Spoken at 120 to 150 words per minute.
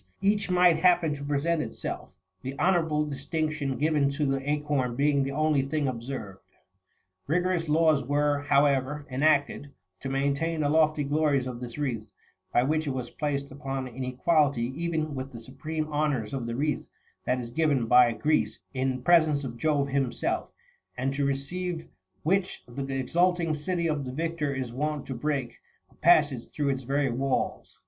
No: average, 165 wpm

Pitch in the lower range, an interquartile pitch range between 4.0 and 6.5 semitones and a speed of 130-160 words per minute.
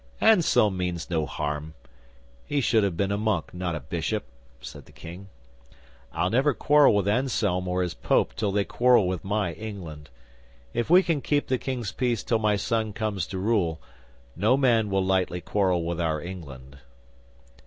No: low, 100 Hz; average, 4.6 semitones; average, 175 wpm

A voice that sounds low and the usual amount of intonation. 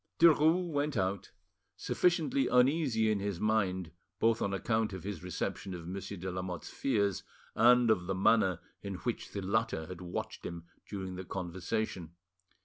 Yes: low, 100 Hz; average, 3.9 semitones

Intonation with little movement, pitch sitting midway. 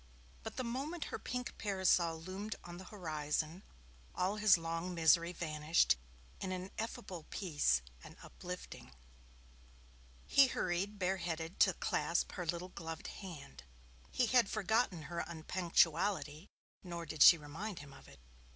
No: average, 3.4 semitones; medium, 175 Hz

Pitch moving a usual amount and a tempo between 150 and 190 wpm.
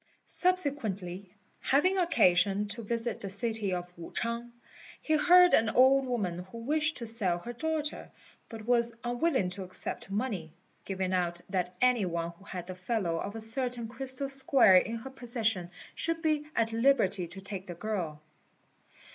No: wide, 5.9 semitones; average, 165 wpm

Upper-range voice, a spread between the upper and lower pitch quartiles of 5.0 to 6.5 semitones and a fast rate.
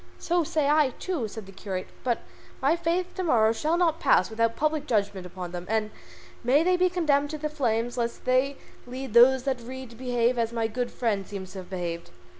Yes: high, 245 Hz; wide, 5.5 semitones; fast, 220 wpm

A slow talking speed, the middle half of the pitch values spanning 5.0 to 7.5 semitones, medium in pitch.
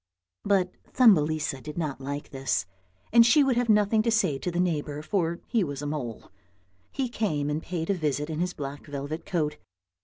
No: average, 190 wpm; wide, 5.6 semitones; medium, 160 Hz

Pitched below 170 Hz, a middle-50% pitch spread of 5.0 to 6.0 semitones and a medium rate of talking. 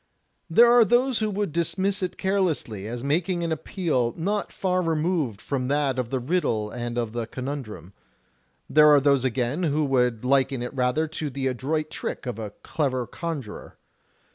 Yes: medium, 140 Hz; wide, 5.6 semitones; average, 170 wpm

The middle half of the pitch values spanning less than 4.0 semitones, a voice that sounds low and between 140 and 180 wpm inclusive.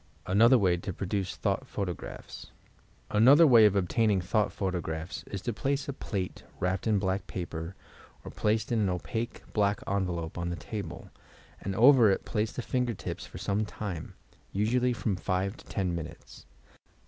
Yes: average, 3.6 semitones; low, 100 Hz; average, 170 wpm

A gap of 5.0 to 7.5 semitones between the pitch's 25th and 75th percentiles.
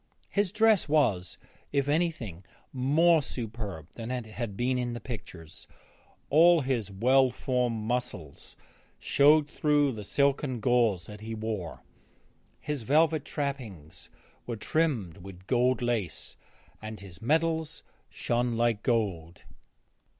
Yes: average, 5.3 semitones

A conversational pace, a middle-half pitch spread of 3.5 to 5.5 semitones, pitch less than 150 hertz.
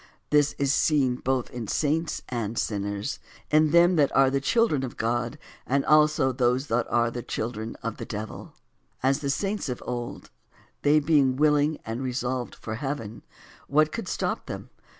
Yes: average, 175 wpm; average, 3.8 semitones; low, 135 Hz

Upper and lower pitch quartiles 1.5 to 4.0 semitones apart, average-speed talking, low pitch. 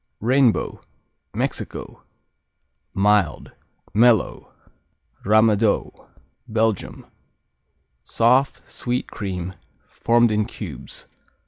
No: average, 2.7 semitones; slow, 65 wpm; low, 110 Hz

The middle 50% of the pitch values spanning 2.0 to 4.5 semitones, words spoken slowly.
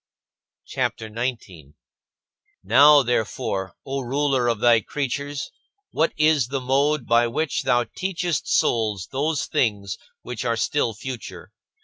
Yes: average, 4.1 semitones; slow, 125 wpm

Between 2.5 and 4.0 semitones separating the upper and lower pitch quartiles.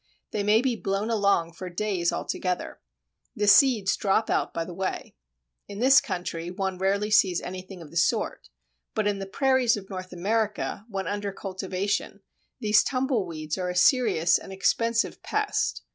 Yes: average, 2.8 semitones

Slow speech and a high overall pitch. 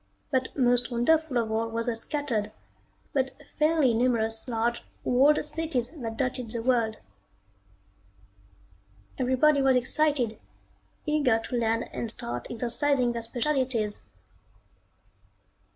Yes: slow, 110 wpm; high, 245 Hz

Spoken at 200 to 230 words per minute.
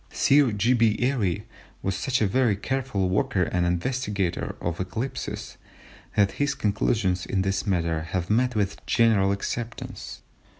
No: average, 140 wpm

